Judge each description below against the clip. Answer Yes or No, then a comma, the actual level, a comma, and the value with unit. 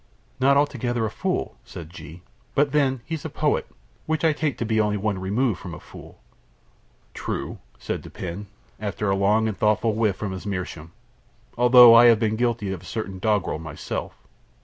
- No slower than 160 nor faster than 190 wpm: Yes, average, 180 wpm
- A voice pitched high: No, low, 110 Hz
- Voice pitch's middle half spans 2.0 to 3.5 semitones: No, average, 4.1 semitones